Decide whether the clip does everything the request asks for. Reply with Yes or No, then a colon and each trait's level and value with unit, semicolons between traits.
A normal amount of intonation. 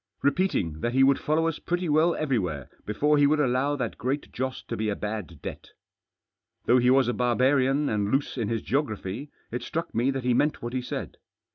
Yes: average, 3.9 semitones